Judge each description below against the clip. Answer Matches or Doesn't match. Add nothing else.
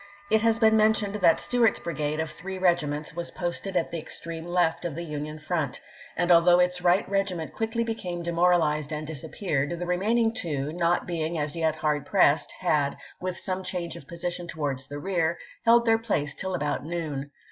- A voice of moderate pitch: Matches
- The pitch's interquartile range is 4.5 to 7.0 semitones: Doesn't match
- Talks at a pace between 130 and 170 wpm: Doesn't match